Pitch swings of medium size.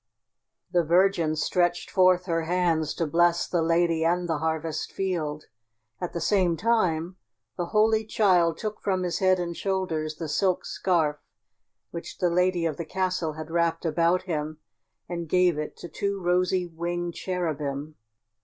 No: narrow, 2.2 semitones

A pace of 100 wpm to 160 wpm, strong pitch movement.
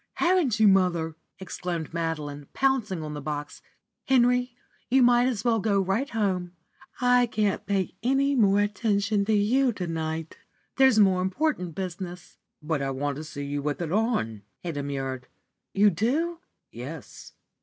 Yes: average, 155 wpm; wide, 6.9 semitones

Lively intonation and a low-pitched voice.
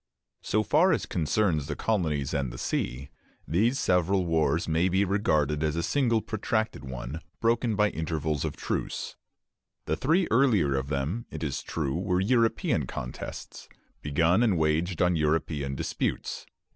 Yes: wide, 6.2 semitones; very low, 85 Hz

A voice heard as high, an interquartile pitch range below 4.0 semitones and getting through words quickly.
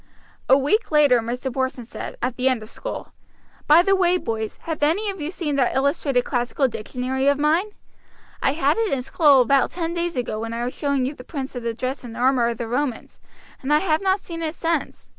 No: very high, 275 Hz; average, 4.7 semitones; fast, 225 wpm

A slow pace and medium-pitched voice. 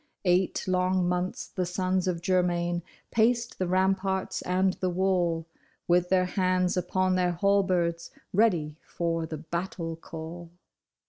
Yes: slow, 130 wpm; medium, 180 Hz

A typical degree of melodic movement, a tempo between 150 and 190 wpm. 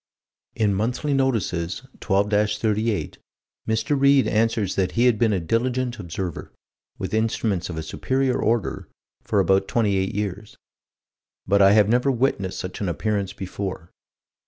No: average, 3.7 semitones; average, 140 wpm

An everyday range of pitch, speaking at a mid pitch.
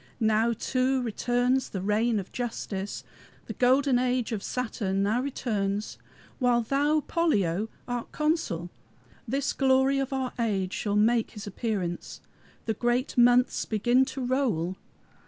No: average, 3.9 semitones; high, 240 Hz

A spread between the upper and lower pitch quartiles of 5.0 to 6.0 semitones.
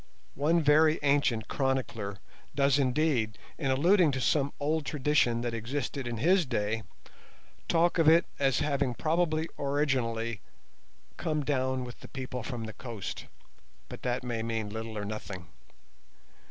No: average, 4.4 semitones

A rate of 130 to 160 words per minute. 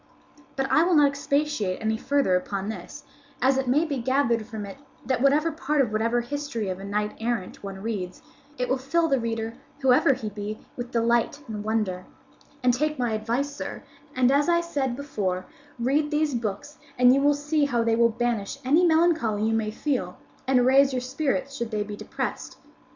No: average, 195 wpm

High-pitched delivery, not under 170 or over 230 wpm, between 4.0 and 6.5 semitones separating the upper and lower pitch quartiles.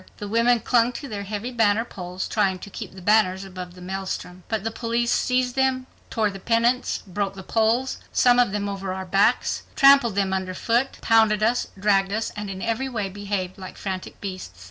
No: high, 210 Hz; average, 195 wpm; average, 3.5 semitones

